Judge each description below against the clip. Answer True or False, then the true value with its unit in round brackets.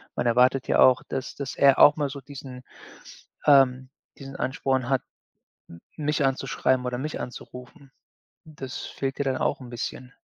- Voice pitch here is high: False (135 Hz)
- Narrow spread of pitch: True (1.7 semitones)